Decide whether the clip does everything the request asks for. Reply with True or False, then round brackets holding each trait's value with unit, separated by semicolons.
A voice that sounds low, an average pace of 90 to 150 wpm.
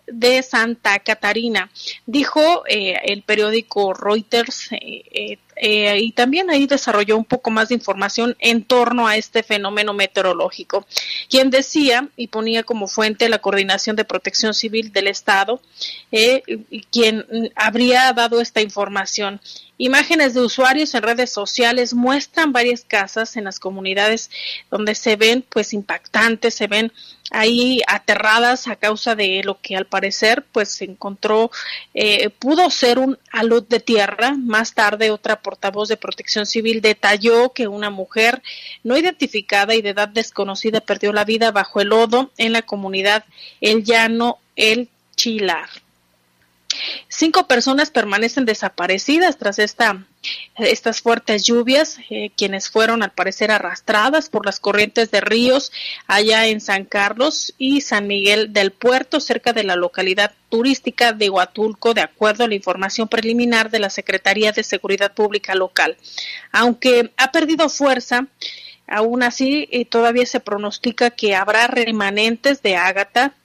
False (225 Hz; 145 wpm)